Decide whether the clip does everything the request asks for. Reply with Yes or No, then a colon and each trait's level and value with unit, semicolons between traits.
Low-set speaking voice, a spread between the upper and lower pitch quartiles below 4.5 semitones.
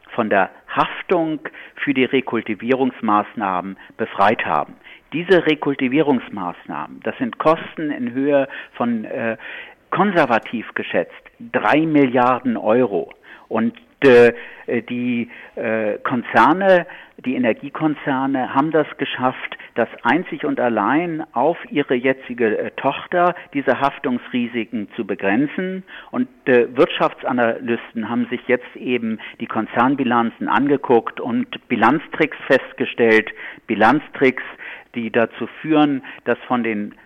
No: low, 130 Hz; average, 5.2 semitones